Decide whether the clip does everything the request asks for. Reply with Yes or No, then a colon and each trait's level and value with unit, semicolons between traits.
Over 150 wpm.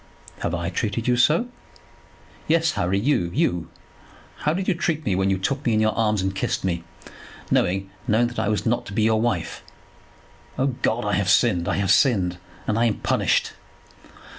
Yes: average, 190 wpm